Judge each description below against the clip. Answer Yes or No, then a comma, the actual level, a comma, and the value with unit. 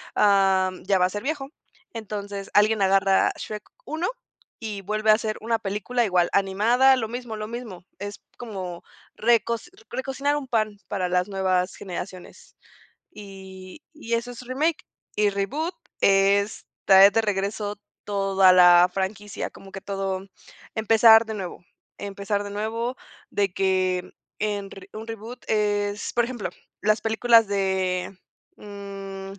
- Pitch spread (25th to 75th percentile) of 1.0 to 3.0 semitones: Yes, average, 2.7 semitones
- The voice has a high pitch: Yes, high, 205 Hz